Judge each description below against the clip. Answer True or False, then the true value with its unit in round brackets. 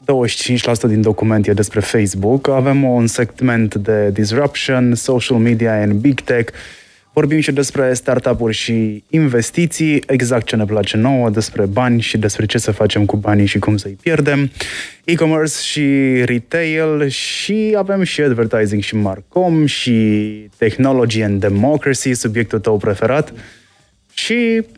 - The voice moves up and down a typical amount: True (4.7 semitones)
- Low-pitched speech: True (120 Hz)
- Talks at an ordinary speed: True (140 wpm)